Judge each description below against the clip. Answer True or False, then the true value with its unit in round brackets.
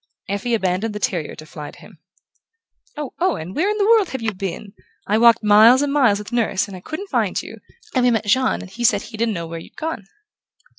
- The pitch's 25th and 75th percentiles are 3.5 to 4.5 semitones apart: False (5.1 semitones)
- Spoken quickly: True (230 wpm)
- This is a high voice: True (225 Hz)